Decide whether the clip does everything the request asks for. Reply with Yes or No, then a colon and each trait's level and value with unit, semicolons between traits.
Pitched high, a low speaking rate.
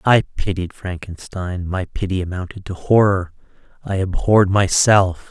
No: very low, 95 Hz; slow, 125 wpm